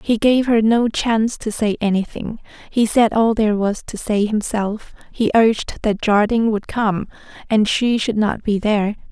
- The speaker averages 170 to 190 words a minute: Yes, average, 185 wpm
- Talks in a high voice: Yes, high, 215 Hz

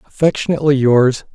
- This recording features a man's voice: Yes, male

